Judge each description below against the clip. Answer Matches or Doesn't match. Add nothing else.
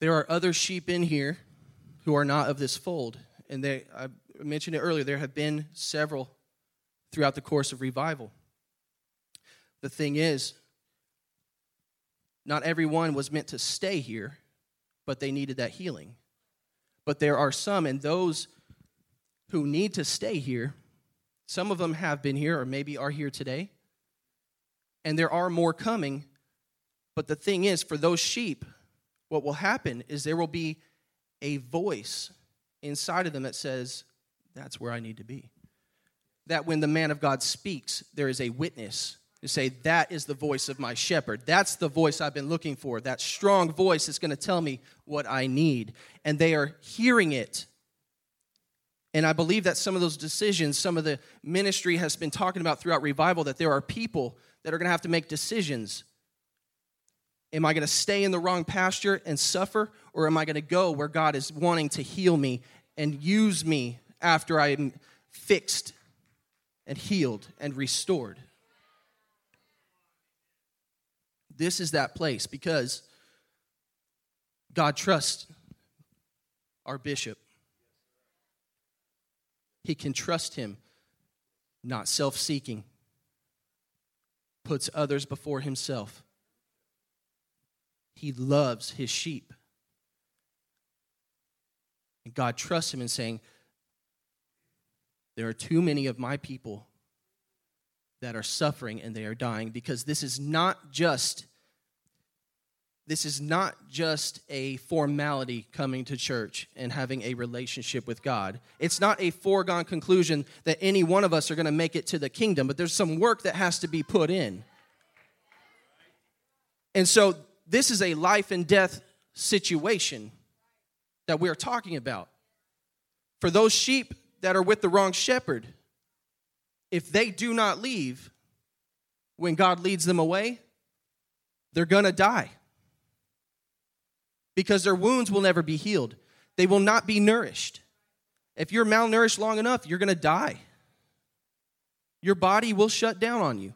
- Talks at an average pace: Matches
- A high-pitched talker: Doesn't match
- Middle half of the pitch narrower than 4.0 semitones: Doesn't match